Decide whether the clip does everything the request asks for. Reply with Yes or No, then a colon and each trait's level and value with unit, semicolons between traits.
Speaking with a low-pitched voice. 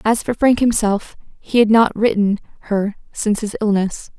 No: high, 215 Hz